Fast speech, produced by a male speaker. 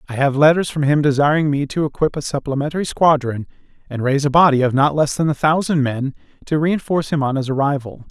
Yes: fast, 215 wpm; male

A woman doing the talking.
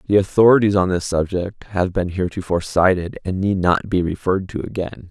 No: male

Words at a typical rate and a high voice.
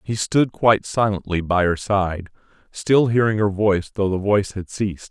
No: average, 190 wpm; low, 100 Hz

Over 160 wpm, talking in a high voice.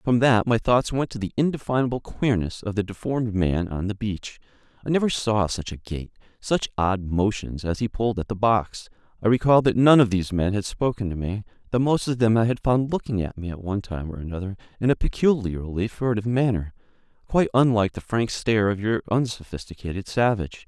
No: fast, 205 wpm; low, 110 Hz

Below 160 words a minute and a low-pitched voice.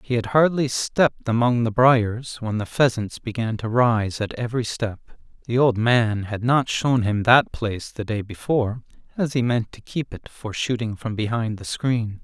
No: average, 195 wpm; low, 115 Hz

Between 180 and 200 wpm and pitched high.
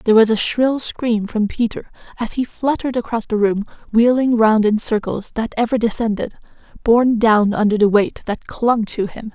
Yes: average, 185 wpm; high, 225 Hz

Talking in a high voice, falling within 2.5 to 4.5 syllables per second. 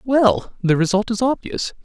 Yes: high, 220 Hz; 4.4 syllables/s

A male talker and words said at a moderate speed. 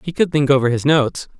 No: male; fast, 260 wpm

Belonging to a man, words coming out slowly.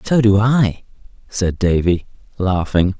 Yes: male; slow, 120 wpm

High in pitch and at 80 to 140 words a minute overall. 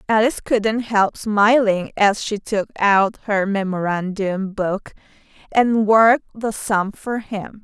Yes: high, 210 Hz; slow, 135 wpm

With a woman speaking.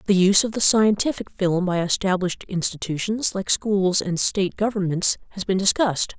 Yes: female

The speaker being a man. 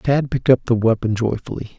Yes: male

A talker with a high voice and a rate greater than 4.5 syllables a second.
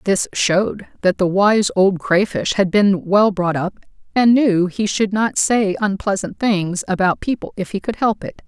No: high, 195 Hz; 4.3 syllables/s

